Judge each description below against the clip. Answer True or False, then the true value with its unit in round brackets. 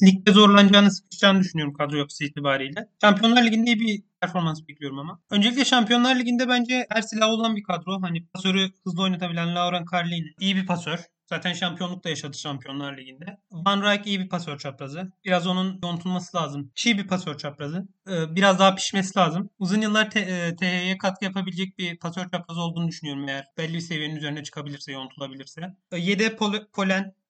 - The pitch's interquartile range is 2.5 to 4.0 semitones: True (3.4 semitones)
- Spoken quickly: True (170 wpm)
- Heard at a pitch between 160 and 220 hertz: True (185 Hz)